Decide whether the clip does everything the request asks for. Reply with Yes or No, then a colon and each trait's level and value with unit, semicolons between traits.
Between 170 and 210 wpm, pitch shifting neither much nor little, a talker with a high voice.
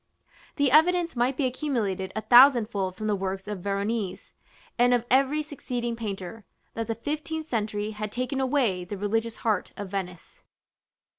No: average, 155 wpm; average, 4.5 semitones; high, 225 Hz